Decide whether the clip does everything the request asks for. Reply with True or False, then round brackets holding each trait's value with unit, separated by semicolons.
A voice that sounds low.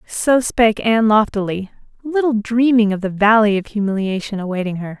False (215 Hz)